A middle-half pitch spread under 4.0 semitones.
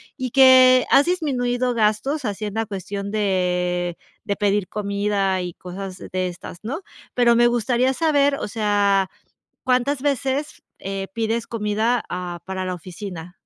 No: average, 4.8 semitones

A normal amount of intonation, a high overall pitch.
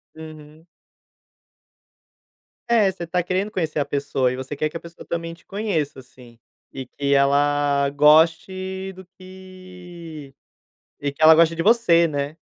No: average, 4.3 semitones; medium, 160 Hz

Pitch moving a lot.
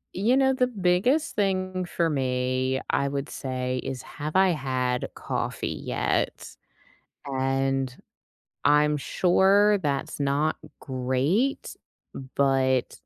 Yes: wide, 6.3 semitones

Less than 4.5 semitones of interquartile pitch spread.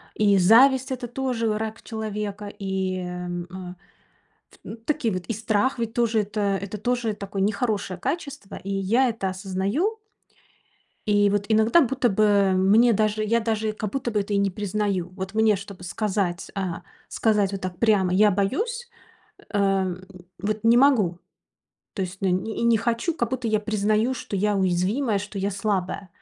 Yes: average, 2.9 semitones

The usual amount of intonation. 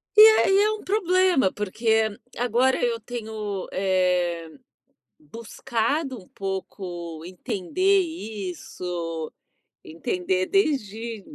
No: wide, 6.4 semitones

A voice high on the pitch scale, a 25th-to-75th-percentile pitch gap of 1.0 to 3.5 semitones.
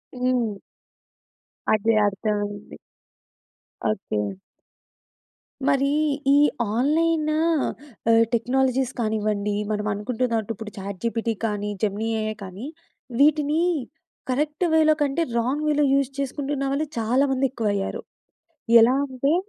No: high, 245 Hz; average, 4.7 semitones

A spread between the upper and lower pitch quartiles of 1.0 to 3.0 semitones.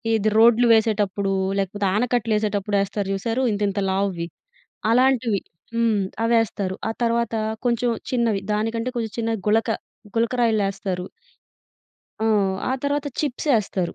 Yes: average, 2.7 semitones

